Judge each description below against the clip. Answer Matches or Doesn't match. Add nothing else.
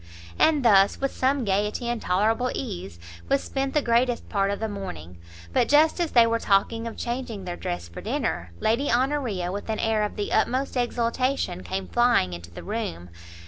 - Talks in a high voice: Matches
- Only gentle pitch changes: Doesn't match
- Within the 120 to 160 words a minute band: Doesn't match